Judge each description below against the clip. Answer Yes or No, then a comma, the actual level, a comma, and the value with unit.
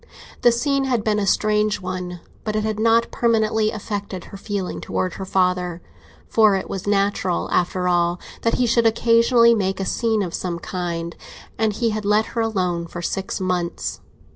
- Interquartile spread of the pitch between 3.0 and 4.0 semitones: Yes, average, 3.5 semitones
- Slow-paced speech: No, average, 180 wpm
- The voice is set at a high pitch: Yes, high, 205 Hz